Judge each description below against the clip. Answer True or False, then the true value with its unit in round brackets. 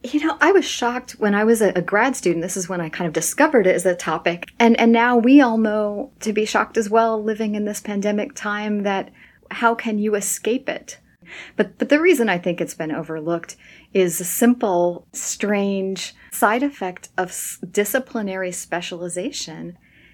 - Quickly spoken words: False (185 wpm)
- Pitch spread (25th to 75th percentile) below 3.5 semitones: False (4.4 semitones)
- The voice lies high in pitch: True (210 Hz)